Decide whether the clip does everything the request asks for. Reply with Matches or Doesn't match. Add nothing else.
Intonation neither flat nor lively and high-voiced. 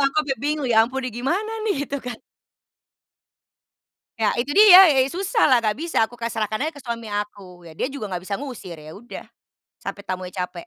Doesn't match